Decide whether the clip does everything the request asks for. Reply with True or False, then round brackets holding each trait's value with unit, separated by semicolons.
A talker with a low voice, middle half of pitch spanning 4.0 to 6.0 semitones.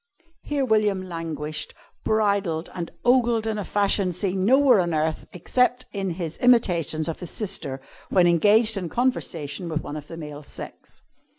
False (185 Hz; 5.0 semitones)